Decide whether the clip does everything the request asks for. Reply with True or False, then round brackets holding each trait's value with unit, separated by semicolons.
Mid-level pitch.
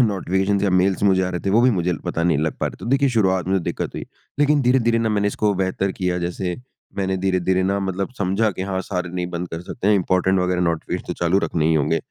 False (95 Hz)